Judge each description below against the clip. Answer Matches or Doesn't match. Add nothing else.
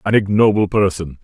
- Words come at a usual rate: Matches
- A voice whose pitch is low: Matches